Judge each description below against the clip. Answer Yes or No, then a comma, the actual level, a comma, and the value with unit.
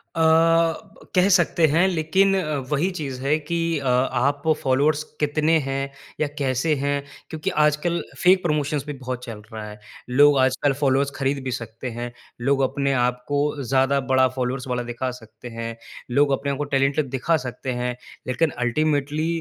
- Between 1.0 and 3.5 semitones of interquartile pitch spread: Yes, average, 2.9 semitones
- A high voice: No, medium, 140 Hz